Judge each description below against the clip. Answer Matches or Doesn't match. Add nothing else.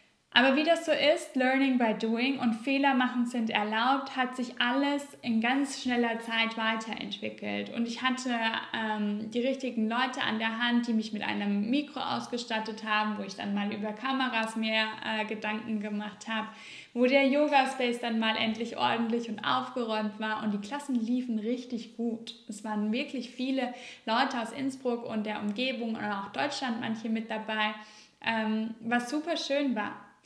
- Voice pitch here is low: Doesn't match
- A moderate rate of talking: Matches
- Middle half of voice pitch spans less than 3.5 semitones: Matches